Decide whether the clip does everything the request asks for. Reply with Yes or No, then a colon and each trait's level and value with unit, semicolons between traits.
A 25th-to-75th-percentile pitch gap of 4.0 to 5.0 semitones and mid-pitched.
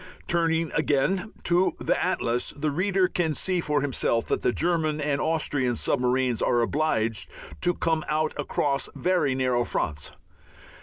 Yes: average, 4.5 semitones; medium, 150 Hz